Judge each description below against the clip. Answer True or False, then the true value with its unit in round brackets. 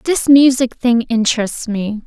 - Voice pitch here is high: True (240 Hz)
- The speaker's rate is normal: True (145 wpm)